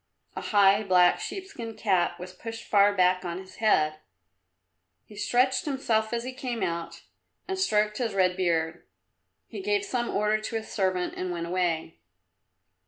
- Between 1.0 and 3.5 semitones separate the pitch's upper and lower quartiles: No, average, 4.4 semitones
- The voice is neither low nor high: No, high, 205 Hz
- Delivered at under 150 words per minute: No, average, 160 wpm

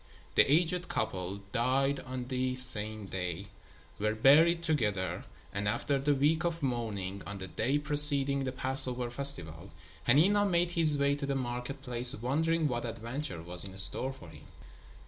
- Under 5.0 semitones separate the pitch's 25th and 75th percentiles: No, wide, 5.6 semitones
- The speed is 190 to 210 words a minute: No, average, 160 wpm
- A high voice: No, low, 130 Hz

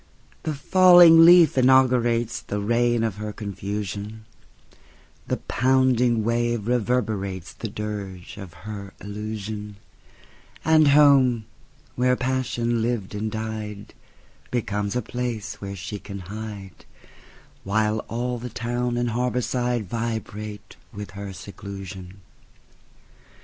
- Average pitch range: Yes, average, 3.2 semitones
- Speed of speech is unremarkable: No, slow, 90 wpm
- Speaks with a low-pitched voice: Yes, low, 110 Hz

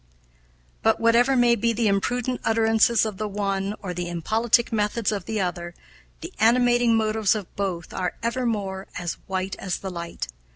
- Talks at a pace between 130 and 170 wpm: Yes, average, 165 wpm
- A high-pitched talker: Yes, high, 215 Hz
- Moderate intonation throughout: Yes, average, 3.3 semitones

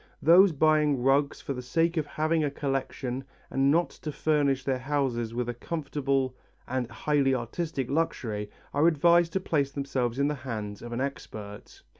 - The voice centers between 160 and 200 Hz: No, medium, 140 Hz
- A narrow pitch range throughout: No, average, 3.3 semitones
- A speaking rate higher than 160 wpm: Yes, average, 170 wpm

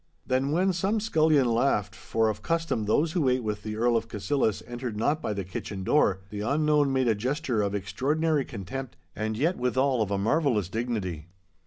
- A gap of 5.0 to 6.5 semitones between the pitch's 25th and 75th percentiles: Yes, wide, 5.6 semitones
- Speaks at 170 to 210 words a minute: Yes, average, 190 wpm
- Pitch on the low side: Yes, low, 125 Hz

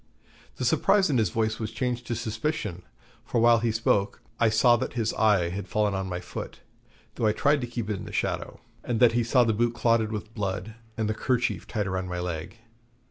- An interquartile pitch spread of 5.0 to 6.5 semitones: No, average, 2.9 semitones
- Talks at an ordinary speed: No, fast, 220 wpm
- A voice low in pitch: Yes, low, 110 Hz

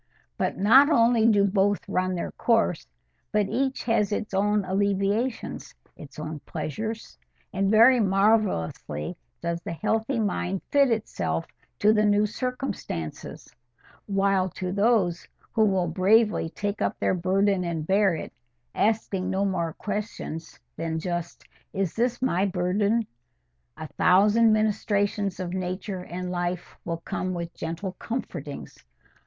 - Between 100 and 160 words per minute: Yes, slow, 135 wpm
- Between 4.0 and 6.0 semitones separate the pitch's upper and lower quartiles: No, average, 3.3 semitones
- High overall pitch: Yes, high, 195 Hz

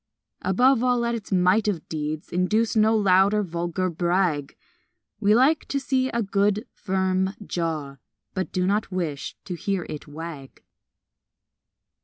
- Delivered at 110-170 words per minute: Yes, average, 145 wpm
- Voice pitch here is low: No, high, 190 Hz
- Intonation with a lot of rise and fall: No, average, 4.0 semitones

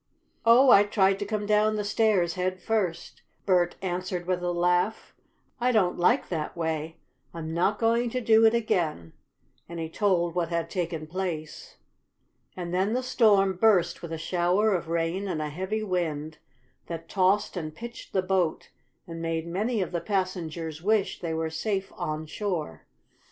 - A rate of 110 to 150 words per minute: No, average, 170 wpm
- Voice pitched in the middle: Yes, medium, 180 Hz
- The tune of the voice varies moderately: Yes, average, 3.8 semitones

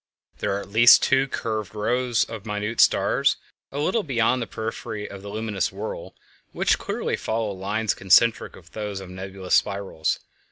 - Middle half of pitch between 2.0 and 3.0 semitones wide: Yes, average, 2.7 semitones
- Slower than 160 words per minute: No, average, 170 wpm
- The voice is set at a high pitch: No, low, 105 Hz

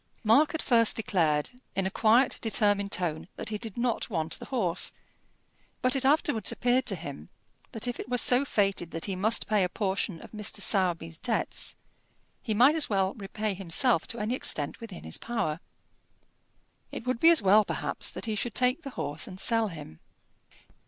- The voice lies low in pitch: No, high, 215 Hz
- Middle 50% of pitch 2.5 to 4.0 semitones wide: No, average, 4.8 semitones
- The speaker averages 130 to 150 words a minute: No, average, 185 wpm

